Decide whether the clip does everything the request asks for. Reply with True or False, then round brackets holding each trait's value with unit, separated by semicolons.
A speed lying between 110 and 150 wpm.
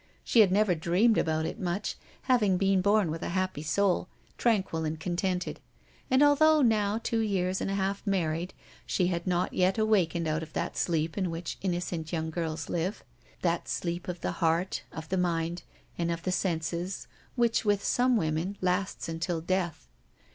False (175 wpm)